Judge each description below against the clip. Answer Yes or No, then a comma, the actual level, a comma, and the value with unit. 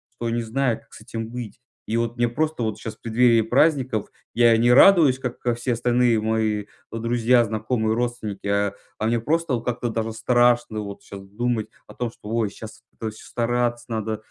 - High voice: No, low, 115 Hz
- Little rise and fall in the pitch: Yes, narrow, 1.8 semitones